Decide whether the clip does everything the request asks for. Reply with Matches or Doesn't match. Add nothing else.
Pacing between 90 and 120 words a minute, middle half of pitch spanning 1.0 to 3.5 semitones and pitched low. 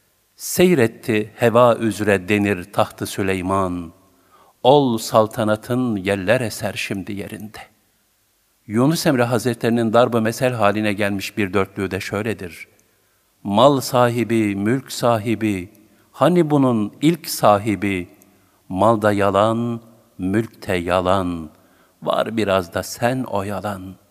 Matches